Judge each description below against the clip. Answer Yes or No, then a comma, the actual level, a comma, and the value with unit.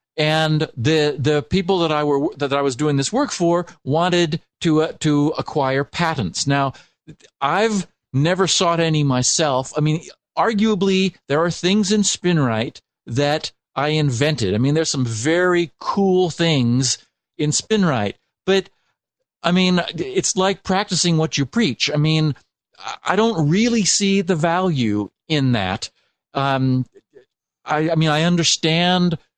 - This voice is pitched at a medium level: Yes, medium, 160 Hz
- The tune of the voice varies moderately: Yes, average, 4.2 semitones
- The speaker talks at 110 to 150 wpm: Yes, average, 145 wpm